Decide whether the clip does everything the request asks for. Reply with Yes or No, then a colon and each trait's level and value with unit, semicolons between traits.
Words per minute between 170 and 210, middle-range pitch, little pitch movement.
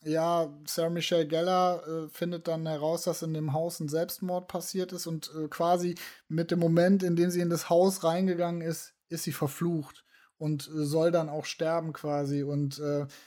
Yes: fast, 190 wpm; medium, 165 Hz; narrow, 1.8 semitones